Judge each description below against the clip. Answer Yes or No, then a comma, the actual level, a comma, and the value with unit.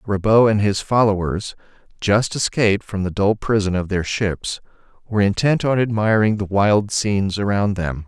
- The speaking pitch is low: Yes, low, 105 Hz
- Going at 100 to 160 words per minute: No, average, 170 wpm